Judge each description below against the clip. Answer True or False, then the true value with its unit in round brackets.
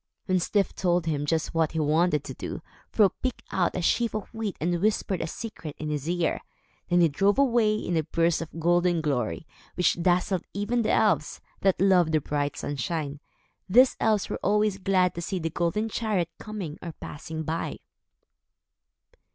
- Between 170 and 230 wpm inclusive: True (180 wpm)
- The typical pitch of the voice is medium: True (175 Hz)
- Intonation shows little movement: False (4.2 semitones)